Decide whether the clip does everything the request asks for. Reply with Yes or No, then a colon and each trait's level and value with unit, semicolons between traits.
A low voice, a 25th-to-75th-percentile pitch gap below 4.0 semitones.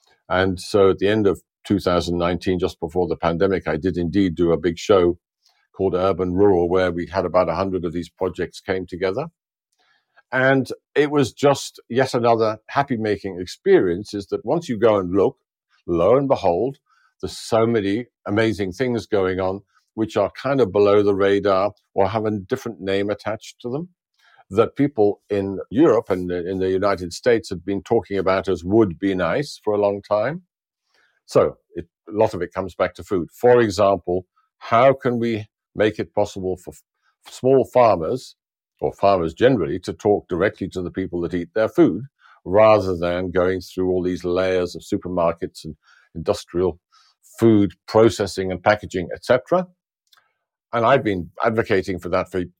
Yes: very low, 95 Hz; average, 3.3 semitones